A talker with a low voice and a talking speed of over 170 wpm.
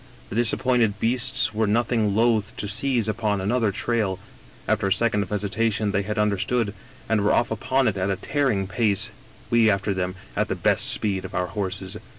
Yes: low, 105 Hz; average, 185 wpm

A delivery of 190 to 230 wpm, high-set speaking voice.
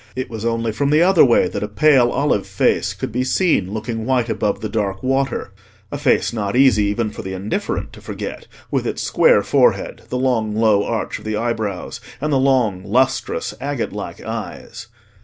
No: average, 195 wpm; low, 115 Hz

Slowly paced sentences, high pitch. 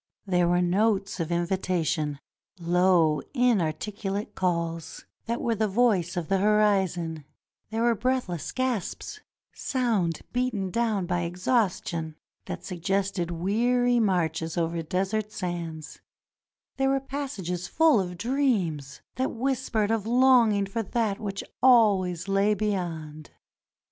Yes: slow, 120 wpm; high, 195 Hz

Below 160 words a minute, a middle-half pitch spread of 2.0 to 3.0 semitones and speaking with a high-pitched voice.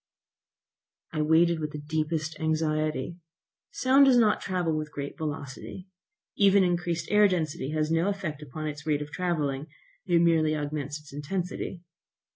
No: average, 145 wpm; average, 2.7 semitones; medium, 155 Hz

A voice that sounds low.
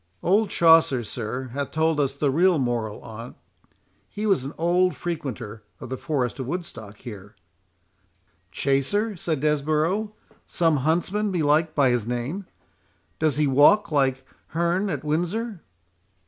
No: medium, 150 Hz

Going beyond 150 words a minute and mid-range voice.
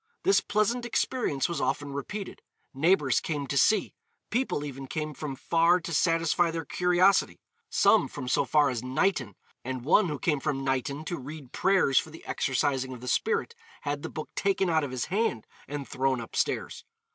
Yes: average, 180 wpm; medium, 150 Hz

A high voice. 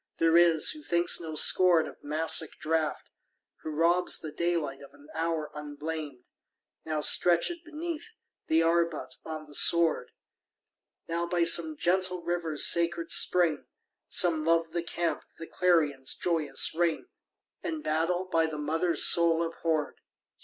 No: medium, 165 Hz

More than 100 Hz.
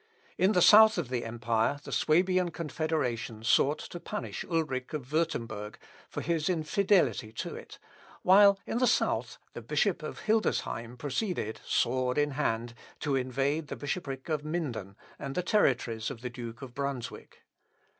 Yes: medium, 140 Hz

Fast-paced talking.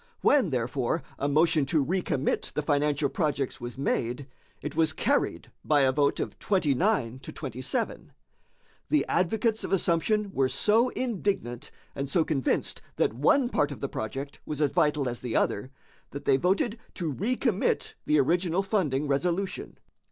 No: average, 155 wpm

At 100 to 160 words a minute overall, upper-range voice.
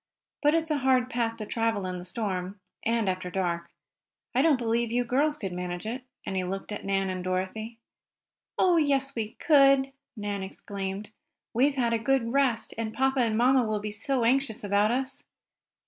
No: average, 185 wpm; high, 230 Hz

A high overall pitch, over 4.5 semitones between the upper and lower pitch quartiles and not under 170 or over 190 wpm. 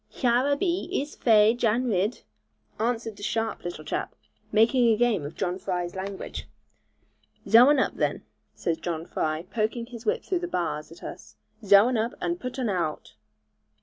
Yes: high, 220 Hz; average, 5.2 semitones; average, 175 wpm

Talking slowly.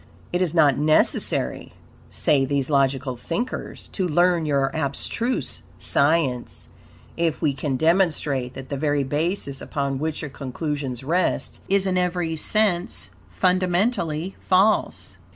Yes: slow, 125 wpm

